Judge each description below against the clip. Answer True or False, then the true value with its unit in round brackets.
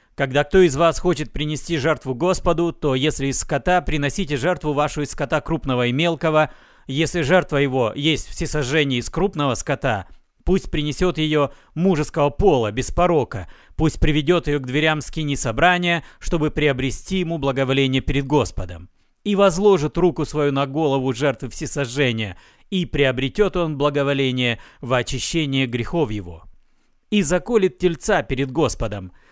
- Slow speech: False (140 wpm)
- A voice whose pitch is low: False (150 Hz)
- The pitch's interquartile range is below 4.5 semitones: True (3.8 semitones)